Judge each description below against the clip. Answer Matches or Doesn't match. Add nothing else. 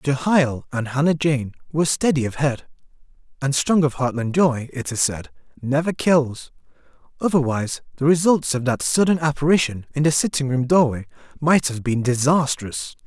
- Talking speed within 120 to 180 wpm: Matches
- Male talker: Matches